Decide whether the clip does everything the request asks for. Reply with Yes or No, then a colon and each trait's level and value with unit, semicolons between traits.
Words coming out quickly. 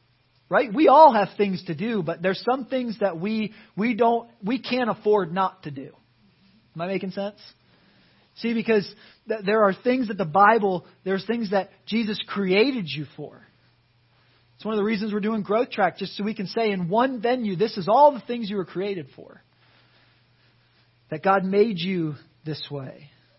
No: average, 185 wpm